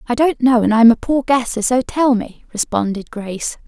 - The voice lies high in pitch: Yes, high, 240 Hz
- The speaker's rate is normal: No, fast, 210 wpm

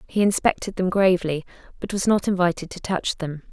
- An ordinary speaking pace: Yes, average, 190 wpm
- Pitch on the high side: No, medium, 180 Hz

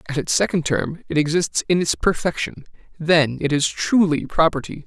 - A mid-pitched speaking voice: Yes, medium, 160 Hz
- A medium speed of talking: Yes, average, 175 wpm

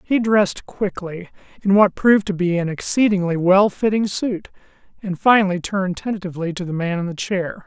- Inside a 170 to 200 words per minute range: Yes, average, 180 wpm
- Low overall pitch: No, high, 190 Hz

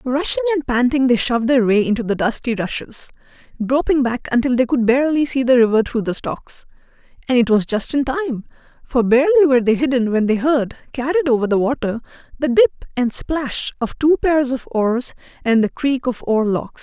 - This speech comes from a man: No, female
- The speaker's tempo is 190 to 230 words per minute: Yes, average, 195 wpm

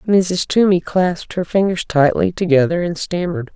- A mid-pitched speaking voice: Yes, medium, 175 Hz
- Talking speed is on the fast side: No, average, 150 wpm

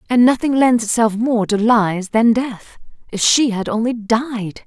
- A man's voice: No, female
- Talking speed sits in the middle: Yes, average, 180 wpm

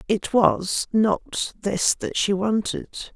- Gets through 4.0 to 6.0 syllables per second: No, 2.8 syllables/s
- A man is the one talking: No, female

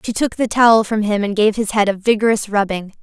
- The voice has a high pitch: Yes, high, 215 Hz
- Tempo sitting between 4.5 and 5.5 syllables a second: No, 5.9 syllables/s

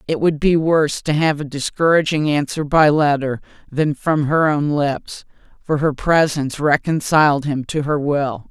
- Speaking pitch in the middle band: Yes, medium, 150 Hz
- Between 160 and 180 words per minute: Yes, average, 170 wpm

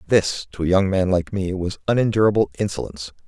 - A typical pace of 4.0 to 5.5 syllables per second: Yes, 5.2 syllables/s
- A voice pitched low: Yes, very low, 95 Hz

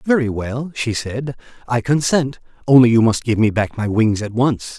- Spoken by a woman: No, male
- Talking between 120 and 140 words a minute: No, average, 200 wpm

